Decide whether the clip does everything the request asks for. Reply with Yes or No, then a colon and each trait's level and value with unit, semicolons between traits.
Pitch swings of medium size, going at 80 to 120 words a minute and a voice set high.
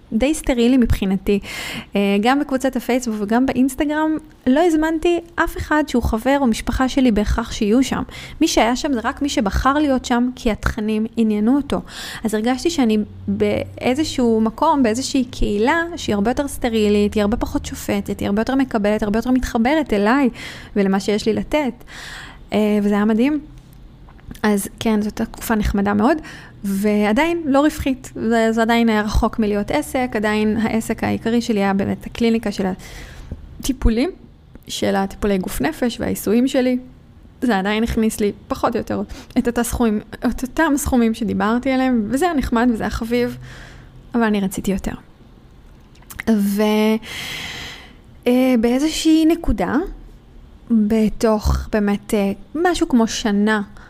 No: average, 3.8 semitones; average, 135 wpm; high, 230 Hz